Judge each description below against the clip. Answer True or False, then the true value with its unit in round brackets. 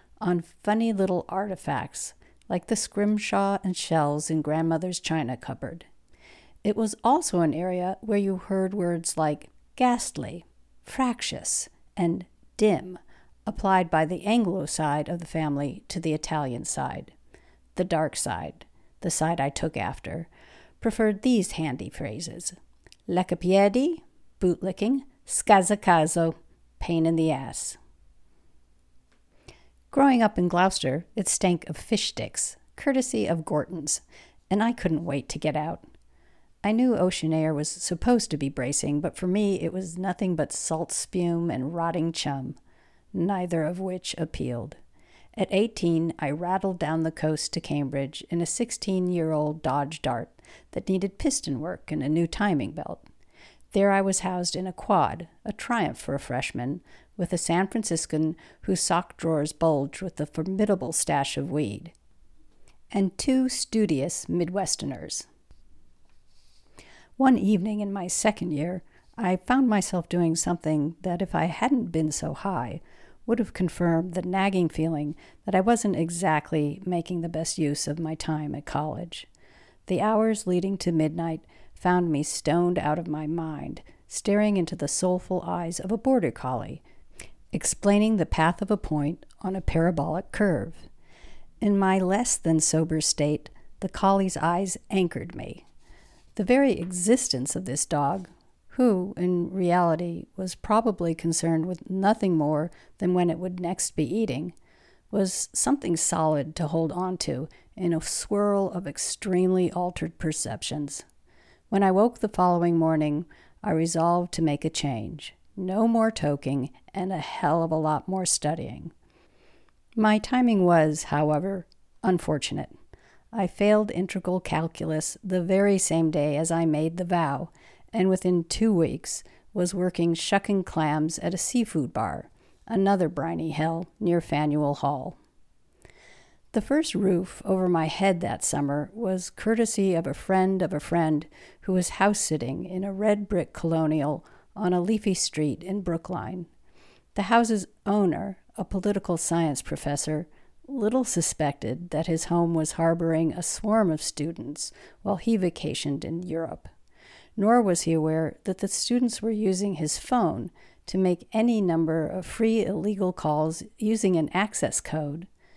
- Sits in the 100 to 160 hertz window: False (175 Hz)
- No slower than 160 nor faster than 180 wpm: False (145 wpm)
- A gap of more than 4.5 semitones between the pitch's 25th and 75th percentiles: False (3.9 semitones)